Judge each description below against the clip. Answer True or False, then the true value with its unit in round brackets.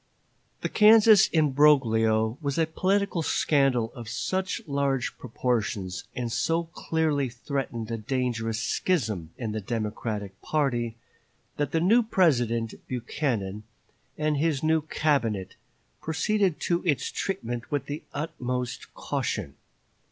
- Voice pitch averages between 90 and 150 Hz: True (135 Hz)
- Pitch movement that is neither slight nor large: False (5.9 semitones)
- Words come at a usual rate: False (115 wpm)